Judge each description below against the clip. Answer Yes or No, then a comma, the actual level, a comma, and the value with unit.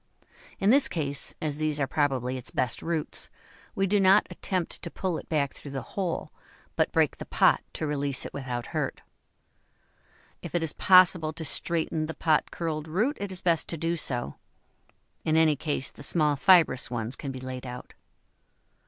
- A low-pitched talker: No, medium, 155 Hz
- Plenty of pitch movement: No, average, 3.7 semitones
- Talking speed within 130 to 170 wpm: No, average, 180 wpm